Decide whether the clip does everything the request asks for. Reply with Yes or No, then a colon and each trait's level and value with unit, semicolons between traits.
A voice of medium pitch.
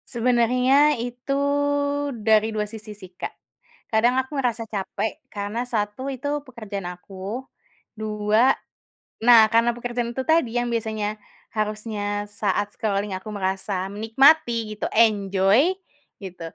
No: high, 220 Hz